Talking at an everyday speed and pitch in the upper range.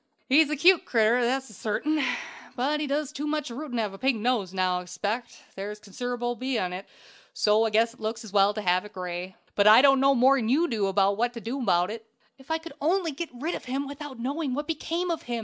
No: fast, 240 wpm; high, 245 Hz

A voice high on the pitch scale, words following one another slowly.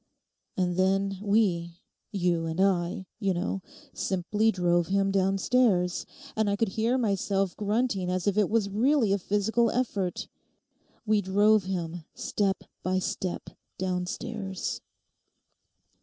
Yes: high, 195 Hz; slow, 115 wpm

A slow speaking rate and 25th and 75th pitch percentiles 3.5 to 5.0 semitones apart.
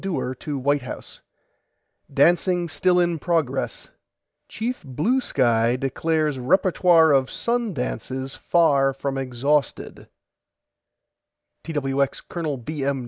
Yes: slow, 105 wpm; average, 4.4 semitones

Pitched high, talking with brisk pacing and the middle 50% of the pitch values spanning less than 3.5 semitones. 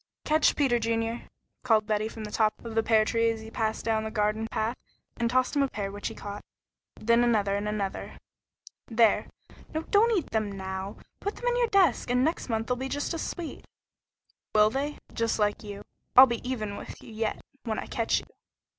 Yes: high, 225 Hz; fast, 210 wpm; average, 3.1 semitones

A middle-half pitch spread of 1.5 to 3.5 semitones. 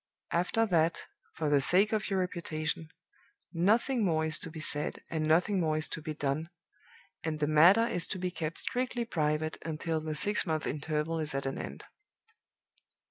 Yes: average, 2.9 semitones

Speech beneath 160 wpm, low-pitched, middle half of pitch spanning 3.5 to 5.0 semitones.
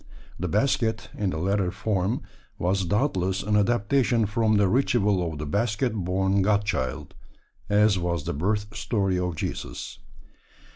No: average, 145 wpm; low, 100 Hz; average, 2.8 semitones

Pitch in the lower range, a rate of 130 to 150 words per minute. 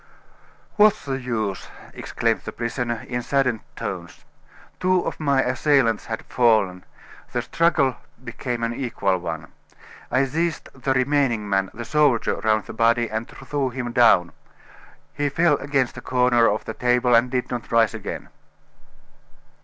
Yes: low, 125 Hz; average, 145 wpm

